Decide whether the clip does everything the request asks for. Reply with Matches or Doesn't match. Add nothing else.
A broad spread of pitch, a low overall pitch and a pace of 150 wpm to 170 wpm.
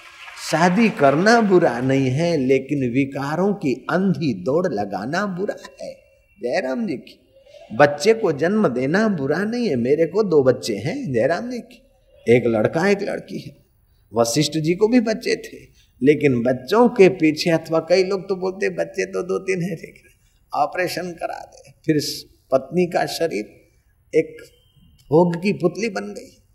Doesn't match